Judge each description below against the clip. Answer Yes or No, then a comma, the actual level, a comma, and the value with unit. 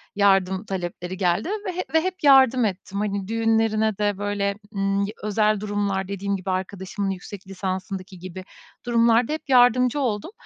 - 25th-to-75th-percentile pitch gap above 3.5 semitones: No, average, 2.9 semitones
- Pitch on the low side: No, high, 200 Hz